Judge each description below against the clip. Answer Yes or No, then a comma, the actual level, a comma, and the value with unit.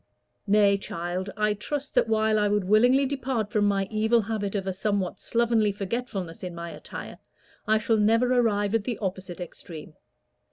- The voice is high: Yes, high, 210 Hz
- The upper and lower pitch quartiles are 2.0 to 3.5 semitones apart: Yes, average, 2.7 semitones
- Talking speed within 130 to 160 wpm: No, average, 170 wpm